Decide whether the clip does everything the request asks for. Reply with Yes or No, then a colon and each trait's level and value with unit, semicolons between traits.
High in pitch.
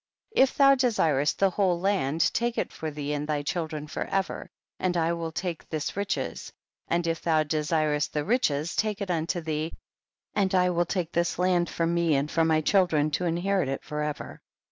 No: medium, 165 Hz